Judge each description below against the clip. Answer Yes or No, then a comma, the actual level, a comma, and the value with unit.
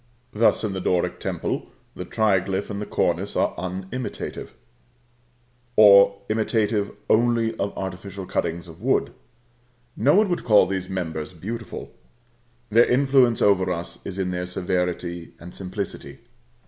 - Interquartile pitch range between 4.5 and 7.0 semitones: No, average, 3.4 semitones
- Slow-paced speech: Yes, slow, 130 wpm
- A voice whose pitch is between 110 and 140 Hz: No, low, 100 Hz